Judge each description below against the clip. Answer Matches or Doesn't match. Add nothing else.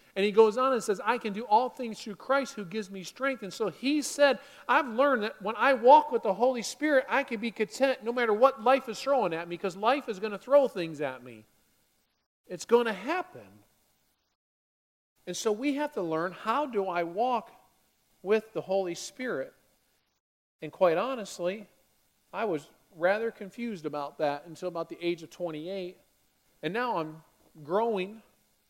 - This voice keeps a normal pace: Matches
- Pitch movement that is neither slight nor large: Doesn't match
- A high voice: Matches